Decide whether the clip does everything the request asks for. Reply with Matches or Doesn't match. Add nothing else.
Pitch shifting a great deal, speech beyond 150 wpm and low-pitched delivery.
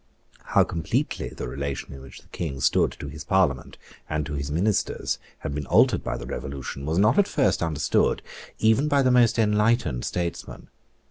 Matches